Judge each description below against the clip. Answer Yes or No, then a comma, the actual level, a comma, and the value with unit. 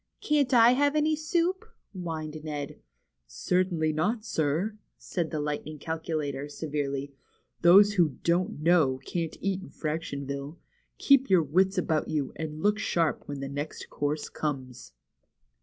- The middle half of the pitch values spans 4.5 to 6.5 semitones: Yes, average, 4.8 semitones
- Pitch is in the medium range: Yes, medium, 160 Hz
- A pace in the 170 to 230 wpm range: No, average, 150 wpm